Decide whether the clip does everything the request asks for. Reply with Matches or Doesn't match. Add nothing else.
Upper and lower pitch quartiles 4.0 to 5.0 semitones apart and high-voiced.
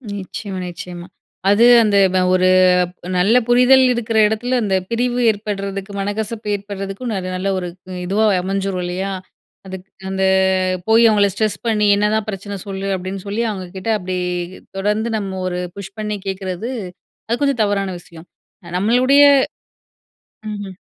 Doesn't match